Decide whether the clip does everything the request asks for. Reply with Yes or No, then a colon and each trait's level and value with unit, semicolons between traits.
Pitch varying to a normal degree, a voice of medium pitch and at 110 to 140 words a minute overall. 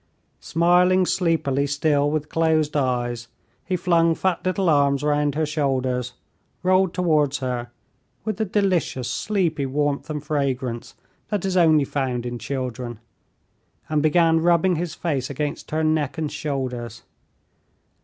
Yes: average, 4.2 semitones; medium, 150 Hz; slow, 135 wpm